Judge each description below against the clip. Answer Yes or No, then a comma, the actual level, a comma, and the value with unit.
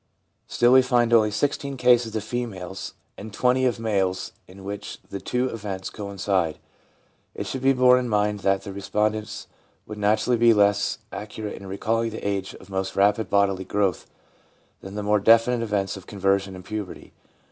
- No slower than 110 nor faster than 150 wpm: No, average, 170 wpm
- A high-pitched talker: No, low, 105 Hz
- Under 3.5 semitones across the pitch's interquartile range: Yes, average, 2.8 semitones